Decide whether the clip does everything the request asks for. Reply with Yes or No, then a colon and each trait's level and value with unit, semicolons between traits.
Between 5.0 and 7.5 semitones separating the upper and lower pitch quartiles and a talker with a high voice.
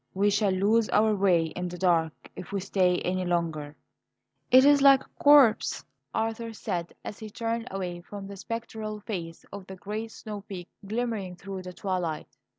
No: average, 3.5 semitones; high, 200 Hz